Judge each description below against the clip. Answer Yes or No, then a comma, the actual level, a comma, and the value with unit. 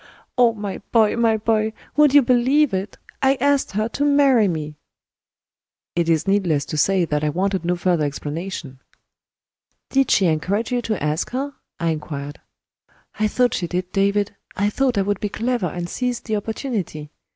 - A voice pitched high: Yes, high, 205 Hz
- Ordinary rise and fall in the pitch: No, wide, 5.9 semitones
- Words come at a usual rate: Yes, average, 175 wpm